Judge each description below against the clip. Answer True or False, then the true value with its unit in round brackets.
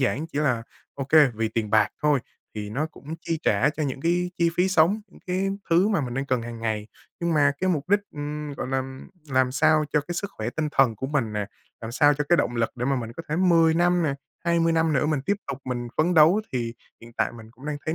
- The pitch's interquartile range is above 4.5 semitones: True (5.0 semitones)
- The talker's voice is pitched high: False (145 Hz)